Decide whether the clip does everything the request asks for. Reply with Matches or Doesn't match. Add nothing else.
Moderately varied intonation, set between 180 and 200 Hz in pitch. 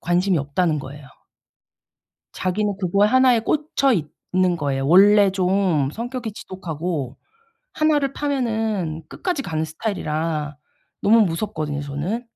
Doesn't match